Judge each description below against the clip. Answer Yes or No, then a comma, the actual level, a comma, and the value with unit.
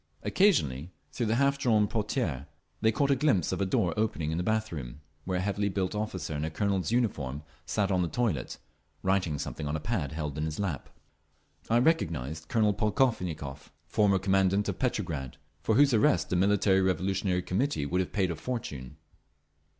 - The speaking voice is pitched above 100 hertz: No, very low, 95 Hz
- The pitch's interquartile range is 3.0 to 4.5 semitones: No, wide, 5.6 semitones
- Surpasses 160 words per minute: Yes, average, 180 wpm